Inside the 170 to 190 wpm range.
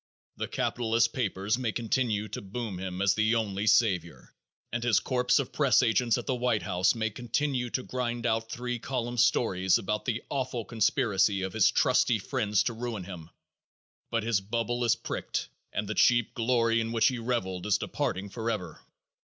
Yes: average, 180 wpm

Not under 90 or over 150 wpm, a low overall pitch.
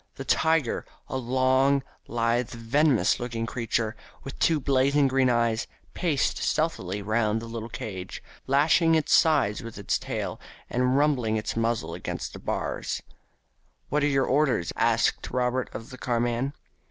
Yes: average, 145 wpm; low, 125 Hz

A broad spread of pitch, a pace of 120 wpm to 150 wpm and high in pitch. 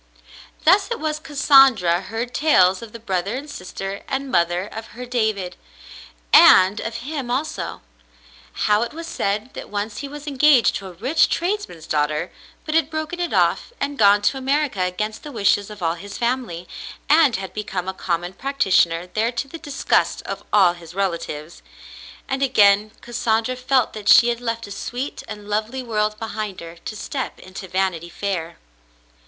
No: wide, 6.1 semitones; average, 170 wpm; high, 215 Hz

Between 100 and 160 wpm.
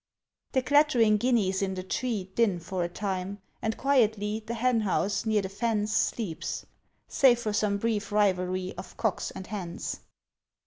Yes: average, 150 wpm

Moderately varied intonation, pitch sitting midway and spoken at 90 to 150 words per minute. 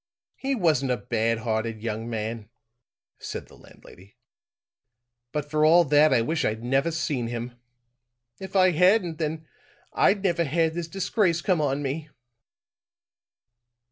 No: wide, 6.3 semitones; medium, 150 Hz; average, 140 wpm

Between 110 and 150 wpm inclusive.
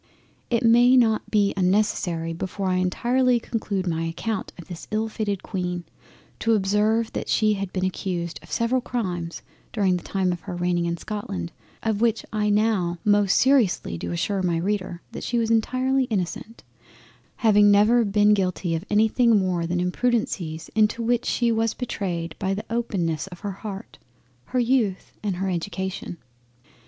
No: average, 165 wpm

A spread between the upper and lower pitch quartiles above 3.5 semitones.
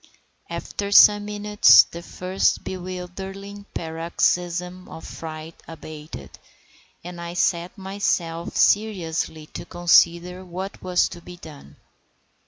No: narrow, 2.4 semitones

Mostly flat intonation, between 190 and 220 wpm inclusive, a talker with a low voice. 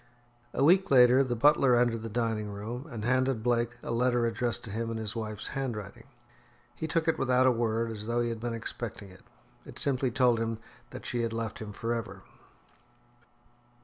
Yes: narrow, 1.9 semitones; average, 195 wpm; low, 120 Hz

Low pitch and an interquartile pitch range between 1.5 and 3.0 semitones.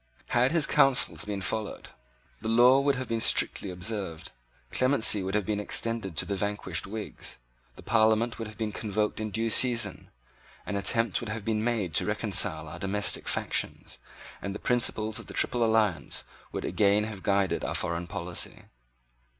Yes: low, 105 Hz; average, 2.7 semitones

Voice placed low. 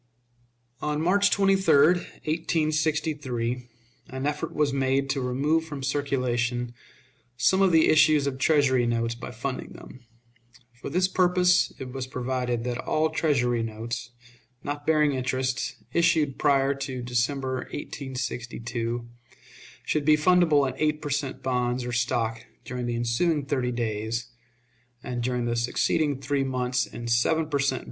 Yes: low, 130 Hz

